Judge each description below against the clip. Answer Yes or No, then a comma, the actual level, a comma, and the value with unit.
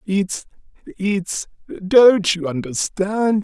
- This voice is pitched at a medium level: No, high, 195 Hz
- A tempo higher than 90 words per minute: No, slow, 50 wpm